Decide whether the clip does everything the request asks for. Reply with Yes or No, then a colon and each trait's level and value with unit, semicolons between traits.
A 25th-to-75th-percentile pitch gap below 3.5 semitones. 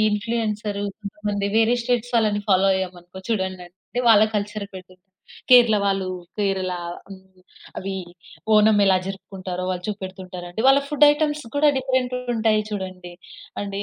Yes: average, 2.9 semitones